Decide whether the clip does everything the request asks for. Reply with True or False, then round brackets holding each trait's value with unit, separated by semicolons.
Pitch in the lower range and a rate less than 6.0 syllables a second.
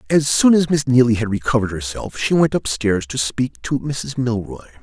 True (120 Hz; 5.2 syllables/s)